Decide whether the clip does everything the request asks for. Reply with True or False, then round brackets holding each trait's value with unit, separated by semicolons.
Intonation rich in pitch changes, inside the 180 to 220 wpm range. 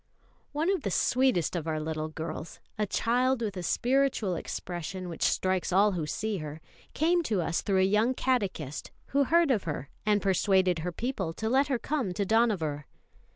True (6.5 semitones; 185 wpm)